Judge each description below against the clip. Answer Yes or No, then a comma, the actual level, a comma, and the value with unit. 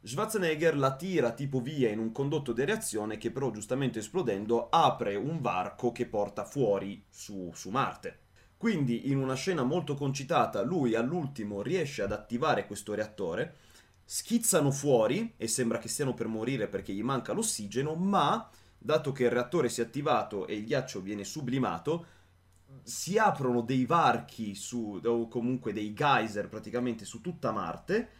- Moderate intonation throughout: Yes, average, 5.0 semitones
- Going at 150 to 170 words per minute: Yes, average, 155 wpm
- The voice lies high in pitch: No, low, 125 Hz